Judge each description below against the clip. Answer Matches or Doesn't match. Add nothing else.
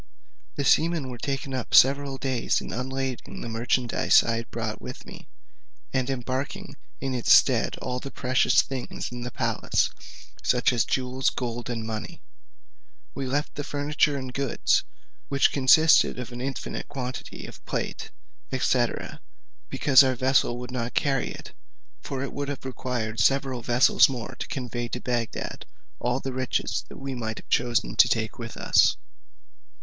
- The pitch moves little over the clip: Matches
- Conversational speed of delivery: Matches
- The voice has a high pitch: Doesn't match